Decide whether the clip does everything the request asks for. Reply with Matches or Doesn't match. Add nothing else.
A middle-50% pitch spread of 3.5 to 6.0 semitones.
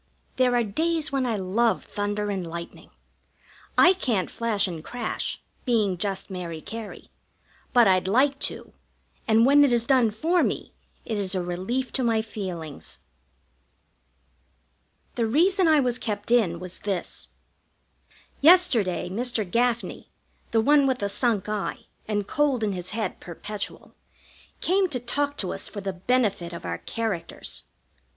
Matches